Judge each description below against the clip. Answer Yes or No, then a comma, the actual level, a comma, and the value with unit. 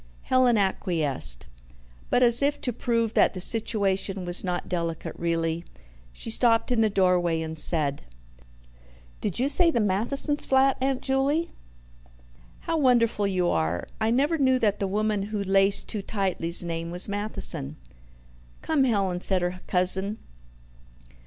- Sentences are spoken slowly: No, average, 145 wpm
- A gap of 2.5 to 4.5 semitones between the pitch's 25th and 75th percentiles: No, wide, 5.4 semitones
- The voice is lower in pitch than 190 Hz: No, high, 200 Hz